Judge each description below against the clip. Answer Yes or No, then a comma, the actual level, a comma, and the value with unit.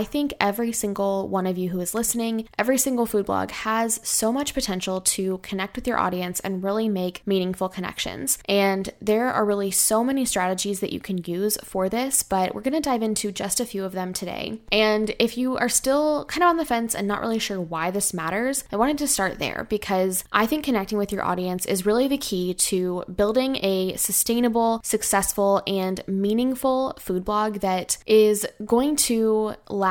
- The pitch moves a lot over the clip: No, average, 3.7 semitones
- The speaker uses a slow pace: No, average, 200 wpm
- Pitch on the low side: No, high, 210 Hz